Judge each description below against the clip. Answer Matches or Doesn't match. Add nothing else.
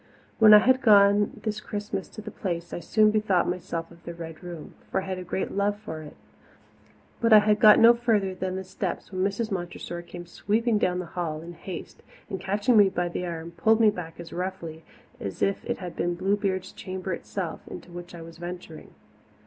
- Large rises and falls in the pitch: Doesn't match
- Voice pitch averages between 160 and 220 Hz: Matches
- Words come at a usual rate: Doesn't match